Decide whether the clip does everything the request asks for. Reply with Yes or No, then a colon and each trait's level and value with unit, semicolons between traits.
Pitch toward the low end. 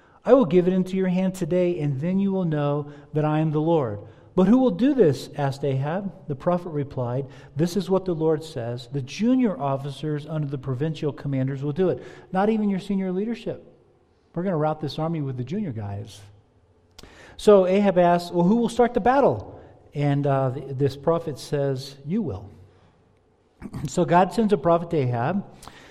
No: medium, 155 Hz